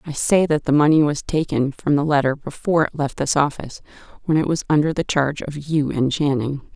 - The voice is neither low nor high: Yes, medium, 145 Hz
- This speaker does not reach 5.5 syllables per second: No, 5.8 syllables/s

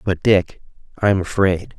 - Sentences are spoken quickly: No, slow, 135 wpm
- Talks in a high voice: No, very low, 95 Hz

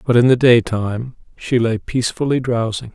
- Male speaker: Yes, male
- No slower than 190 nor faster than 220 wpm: No, average, 165 wpm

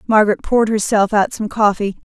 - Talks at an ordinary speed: Yes, average, 170 wpm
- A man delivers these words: No, female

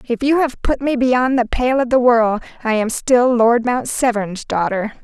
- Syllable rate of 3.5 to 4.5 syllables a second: Yes, 4.4 syllables/s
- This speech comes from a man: No, female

